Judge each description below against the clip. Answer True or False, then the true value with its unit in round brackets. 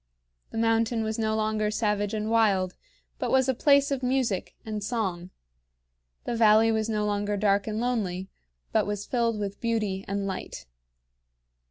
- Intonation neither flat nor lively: False (2.1 semitones)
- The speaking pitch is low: False (215 Hz)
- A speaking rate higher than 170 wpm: False (160 wpm)